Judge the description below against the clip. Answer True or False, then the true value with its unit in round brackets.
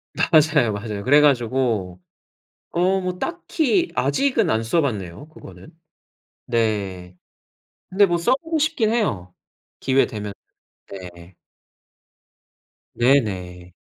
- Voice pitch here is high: False (125 Hz)